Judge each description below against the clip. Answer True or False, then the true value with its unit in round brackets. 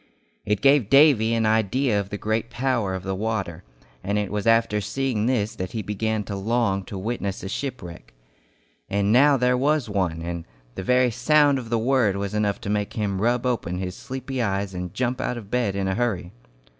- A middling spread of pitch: True (4.1 semitones)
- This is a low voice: True (110 Hz)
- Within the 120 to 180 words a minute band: False (205 wpm)